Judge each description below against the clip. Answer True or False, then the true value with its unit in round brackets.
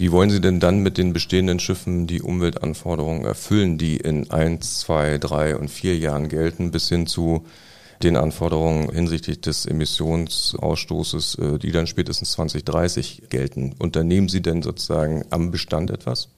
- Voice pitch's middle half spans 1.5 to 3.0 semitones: True (2.5 semitones)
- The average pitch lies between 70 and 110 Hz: True (80 Hz)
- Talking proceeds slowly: False (150 wpm)